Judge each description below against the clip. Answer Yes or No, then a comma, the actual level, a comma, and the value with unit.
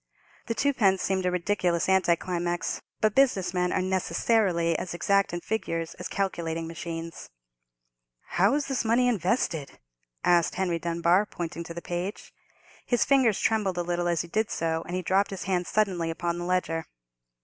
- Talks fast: No, average, 170 wpm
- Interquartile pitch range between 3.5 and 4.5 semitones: No, average, 2.8 semitones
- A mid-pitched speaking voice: Yes, medium, 180 Hz